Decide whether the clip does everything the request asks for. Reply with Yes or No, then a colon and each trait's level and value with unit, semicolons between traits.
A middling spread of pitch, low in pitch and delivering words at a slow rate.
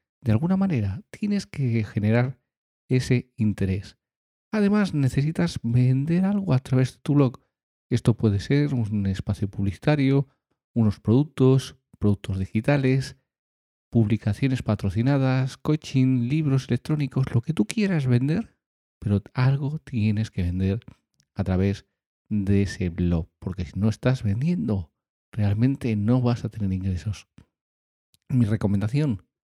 Yes: average, 4.9 semitones; low, 120 Hz; slow, 120 wpm